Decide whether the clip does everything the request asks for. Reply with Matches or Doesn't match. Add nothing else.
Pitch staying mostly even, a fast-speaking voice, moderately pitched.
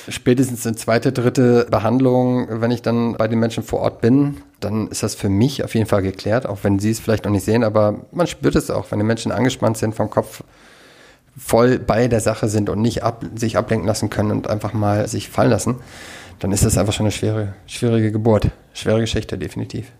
Doesn't match